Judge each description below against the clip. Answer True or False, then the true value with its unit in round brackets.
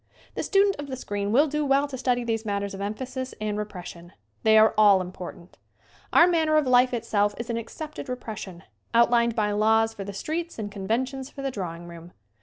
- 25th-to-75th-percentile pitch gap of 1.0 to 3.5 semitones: False (4.5 semitones)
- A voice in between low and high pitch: False (225 Hz)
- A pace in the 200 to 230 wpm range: True (205 wpm)